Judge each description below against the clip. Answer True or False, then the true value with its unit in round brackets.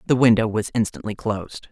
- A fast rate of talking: False (175 wpm)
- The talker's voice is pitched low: True (110 Hz)